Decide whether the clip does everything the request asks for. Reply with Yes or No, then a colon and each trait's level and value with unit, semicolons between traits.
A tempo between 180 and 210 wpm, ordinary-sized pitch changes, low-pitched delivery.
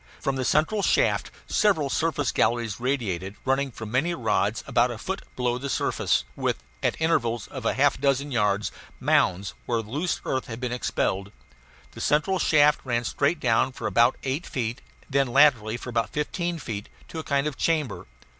Yes: average, 185 wpm; average, 4.2 semitones; low, 130 Hz